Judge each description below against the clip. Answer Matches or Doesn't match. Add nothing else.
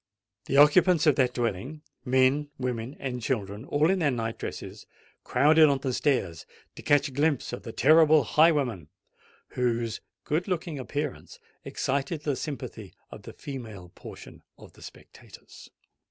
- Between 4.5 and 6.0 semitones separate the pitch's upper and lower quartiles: Doesn't match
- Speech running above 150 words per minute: Doesn't match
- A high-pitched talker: Doesn't match